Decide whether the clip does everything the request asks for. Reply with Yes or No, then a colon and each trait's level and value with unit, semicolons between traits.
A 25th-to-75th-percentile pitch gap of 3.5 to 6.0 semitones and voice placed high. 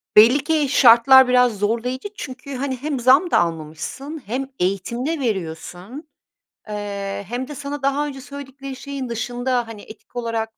Yes: average, 3.9 semitones; very high, 250 Hz